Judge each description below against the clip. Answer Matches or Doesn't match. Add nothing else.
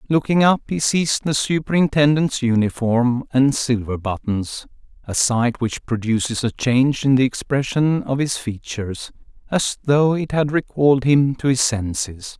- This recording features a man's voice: Matches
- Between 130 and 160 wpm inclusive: Matches